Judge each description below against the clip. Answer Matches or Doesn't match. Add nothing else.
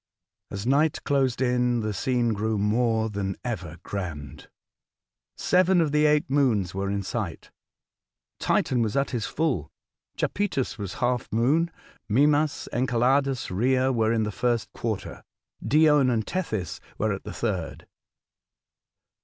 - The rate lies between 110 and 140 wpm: Matches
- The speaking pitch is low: Matches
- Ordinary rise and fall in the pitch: Matches